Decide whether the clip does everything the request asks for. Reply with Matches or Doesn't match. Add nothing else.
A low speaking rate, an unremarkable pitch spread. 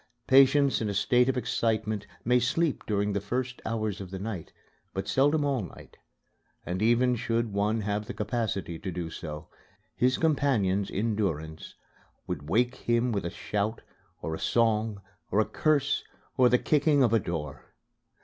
Doesn't match